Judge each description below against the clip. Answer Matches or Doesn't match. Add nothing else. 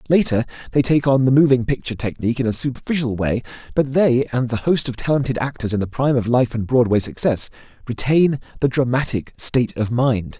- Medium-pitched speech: Doesn't match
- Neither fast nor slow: Matches